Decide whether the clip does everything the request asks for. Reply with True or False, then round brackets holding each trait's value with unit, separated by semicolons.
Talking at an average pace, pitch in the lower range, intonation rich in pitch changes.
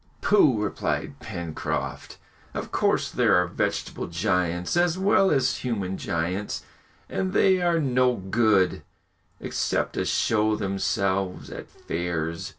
False (120 wpm; 100 Hz; 6.8 semitones)